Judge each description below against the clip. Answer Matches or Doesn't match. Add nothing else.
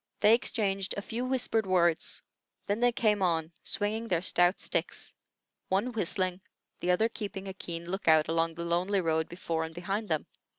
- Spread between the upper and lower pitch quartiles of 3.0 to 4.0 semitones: Matches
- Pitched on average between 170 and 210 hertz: Matches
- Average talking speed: Matches